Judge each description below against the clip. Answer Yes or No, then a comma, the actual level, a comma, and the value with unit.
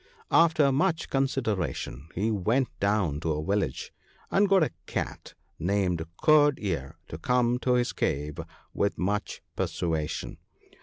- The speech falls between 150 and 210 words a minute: No, slow, 135 wpm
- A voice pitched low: Yes, low, 100 Hz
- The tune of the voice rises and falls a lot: Yes, wide, 8.5 semitones